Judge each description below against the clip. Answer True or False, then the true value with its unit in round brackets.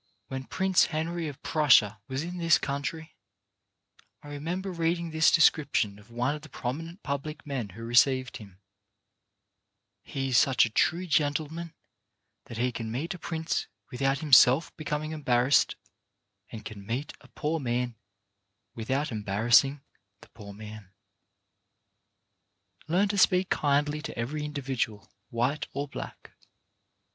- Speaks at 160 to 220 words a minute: False (135 wpm)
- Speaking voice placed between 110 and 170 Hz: True (140 Hz)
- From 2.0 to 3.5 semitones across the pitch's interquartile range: False (4.9 semitones)